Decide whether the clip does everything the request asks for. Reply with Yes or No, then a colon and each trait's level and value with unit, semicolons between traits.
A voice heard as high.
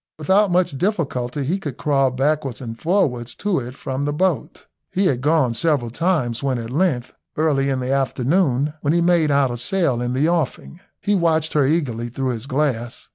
No: medium, 140 Hz